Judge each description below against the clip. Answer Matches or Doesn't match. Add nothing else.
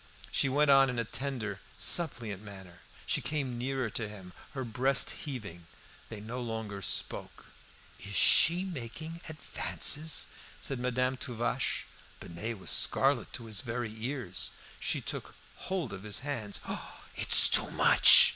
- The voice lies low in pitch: Matches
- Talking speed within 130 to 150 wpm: Matches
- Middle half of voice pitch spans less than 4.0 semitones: Doesn't match